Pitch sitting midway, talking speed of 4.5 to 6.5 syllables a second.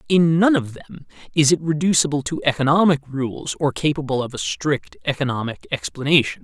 Yes: medium, 145 Hz; 5.3 syllables/s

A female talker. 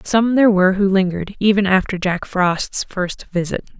Yes: female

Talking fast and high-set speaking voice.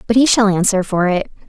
Yes: fast, 245 wpm; high, 205 Hz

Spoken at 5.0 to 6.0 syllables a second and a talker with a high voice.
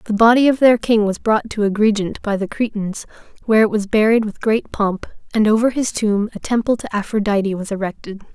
Yes: 5.7 syllables/s; high, 215 Hz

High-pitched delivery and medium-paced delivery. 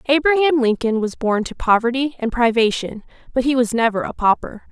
Yes: high, 245 Hz; average, 180 wpm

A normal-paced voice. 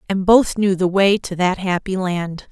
No: fast, 215 wpm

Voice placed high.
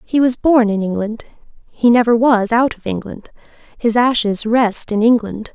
Yes: high, 225 Hz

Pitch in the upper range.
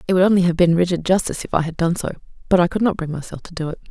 No: medium, 175 Hz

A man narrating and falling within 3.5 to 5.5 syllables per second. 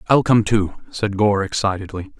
Yes: male; 5.1 syllables/s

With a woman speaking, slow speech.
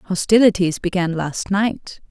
Yes: female; slow, 115 wpm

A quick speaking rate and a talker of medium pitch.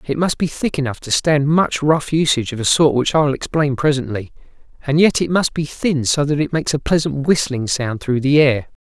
Yes: fast, 240 wpm; medium, 145 Hz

